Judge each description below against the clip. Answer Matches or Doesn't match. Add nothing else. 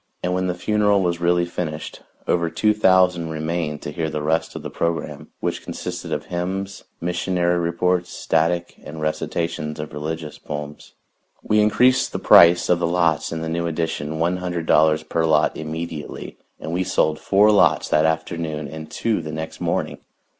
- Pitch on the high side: Doesn't match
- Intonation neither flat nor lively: Doesn't match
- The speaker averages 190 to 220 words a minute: Doesn't match